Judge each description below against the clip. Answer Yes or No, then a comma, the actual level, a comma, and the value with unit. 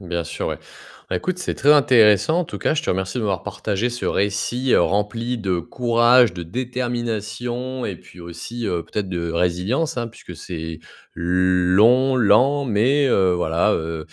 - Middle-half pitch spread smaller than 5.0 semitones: No, wide, 5.6 semitones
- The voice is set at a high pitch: No, low, 110 Hz